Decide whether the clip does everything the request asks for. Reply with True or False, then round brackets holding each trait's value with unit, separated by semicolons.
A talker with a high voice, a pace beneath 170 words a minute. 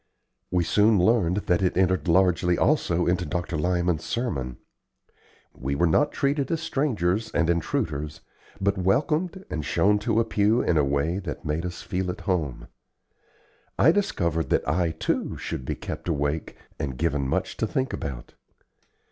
False (90 Hz; 160 wpm)